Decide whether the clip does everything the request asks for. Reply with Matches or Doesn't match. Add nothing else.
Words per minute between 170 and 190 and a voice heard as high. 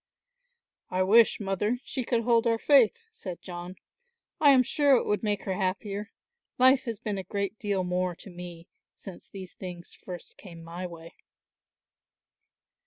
Doesn't match